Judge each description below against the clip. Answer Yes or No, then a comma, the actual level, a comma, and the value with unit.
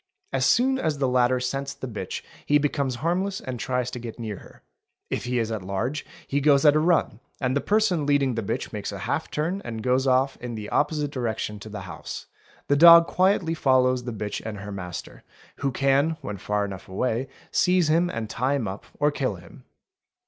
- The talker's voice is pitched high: No, low, 130 Hz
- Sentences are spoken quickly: Yes, fast, 210 wpm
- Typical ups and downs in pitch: Yes, average, 4.8 semitones